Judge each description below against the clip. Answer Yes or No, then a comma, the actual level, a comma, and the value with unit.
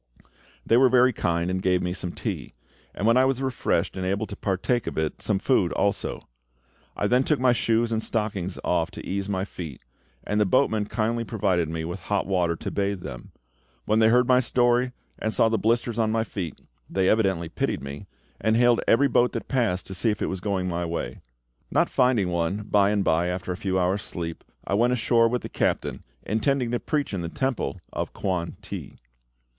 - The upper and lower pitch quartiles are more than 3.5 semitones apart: Yes, average, 4.5 semitones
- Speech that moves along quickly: Yes, fast, 210 wpm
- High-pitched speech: No, low, 105 Hz